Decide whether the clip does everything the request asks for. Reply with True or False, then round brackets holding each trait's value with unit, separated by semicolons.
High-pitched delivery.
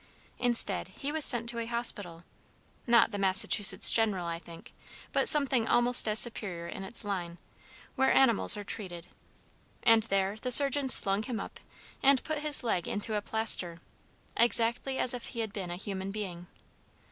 True (220 Hz)